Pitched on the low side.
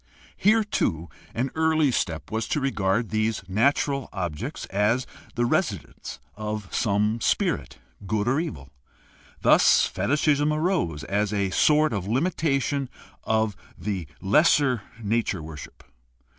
Yes: low, 110 Hz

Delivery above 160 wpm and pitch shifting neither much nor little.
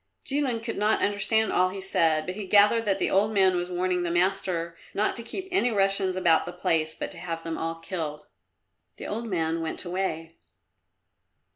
Yes: average, 190 wpm; average, 3.6 semitones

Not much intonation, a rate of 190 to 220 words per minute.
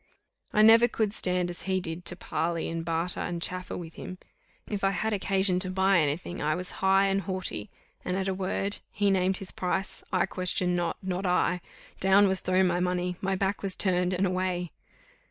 Yes: narrow, 1.5 semitones; fast, 205 wpm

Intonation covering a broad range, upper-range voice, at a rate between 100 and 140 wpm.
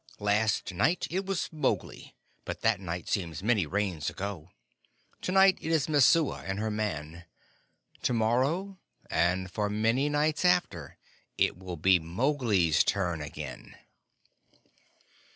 No: wide, 8.6 semitones; low, 105 Hz; slow, 135 wpm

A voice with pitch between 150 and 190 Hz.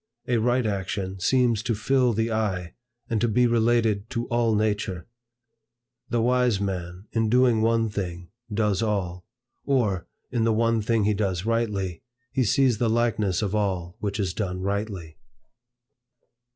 No: low, 110 Hz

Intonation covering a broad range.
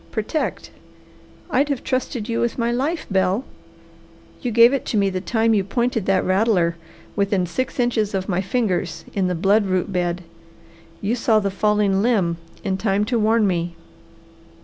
No: average, 3.9 semitones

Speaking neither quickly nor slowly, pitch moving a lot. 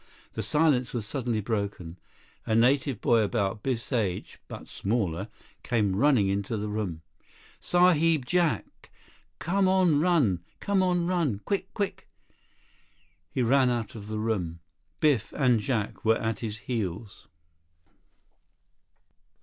No: slow, 125 wpm; wide, 6.1 semitones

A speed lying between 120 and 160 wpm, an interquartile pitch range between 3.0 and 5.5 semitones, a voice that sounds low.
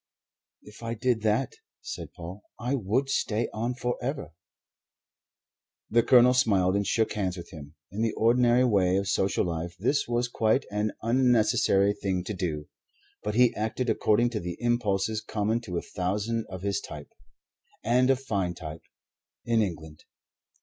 Yes: average, 155 wpm; average, 4.1 semitones; low, 110 Hz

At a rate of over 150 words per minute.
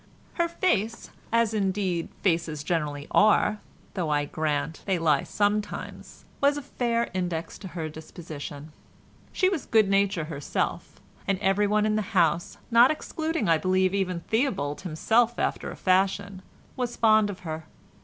No: average, 145 wpm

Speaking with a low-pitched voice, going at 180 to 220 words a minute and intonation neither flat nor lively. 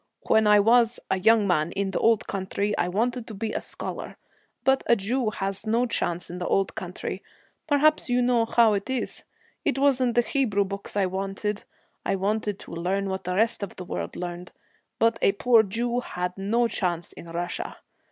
No: high, 210 Hz; average, 195 wpm; average, 3.7 semitones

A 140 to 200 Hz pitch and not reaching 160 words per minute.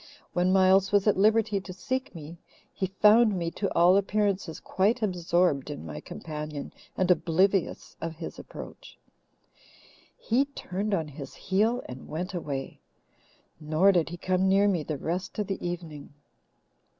Yes: medium, 185 Hz; average, 150 wpm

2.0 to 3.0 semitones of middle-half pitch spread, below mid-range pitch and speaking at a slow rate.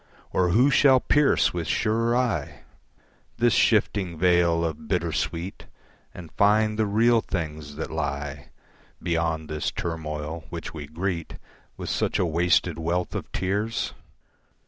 No: average, 5.1 semitones; very low, 85 Hz; slow, 130 wpm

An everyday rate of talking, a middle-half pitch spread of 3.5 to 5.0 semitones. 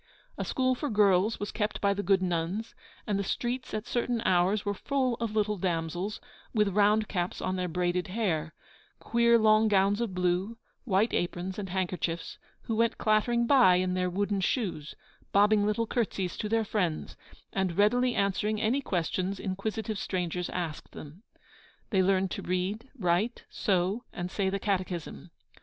No: average, 165 wpm; average, 3.1 semitones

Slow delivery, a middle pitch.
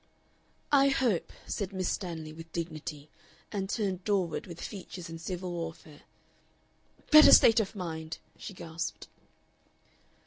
Yes: slow, 125 wpm; medium, 180 Hz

